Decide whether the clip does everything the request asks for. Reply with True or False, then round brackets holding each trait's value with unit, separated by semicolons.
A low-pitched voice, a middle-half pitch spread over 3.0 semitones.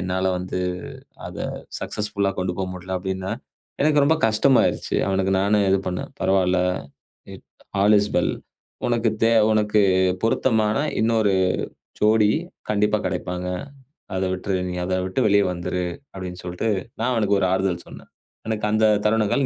False (100 Hz; 2.7 semitones)